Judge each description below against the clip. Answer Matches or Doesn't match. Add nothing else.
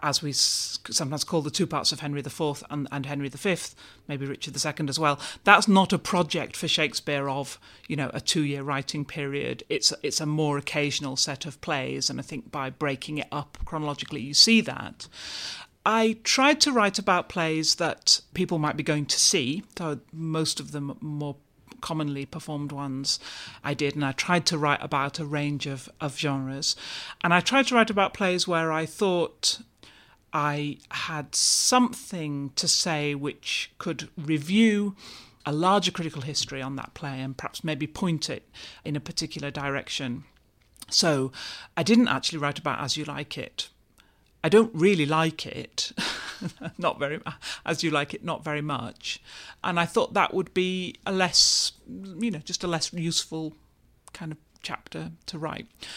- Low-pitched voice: Doesn't match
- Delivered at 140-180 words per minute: Matches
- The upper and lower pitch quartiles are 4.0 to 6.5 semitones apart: Doesn't match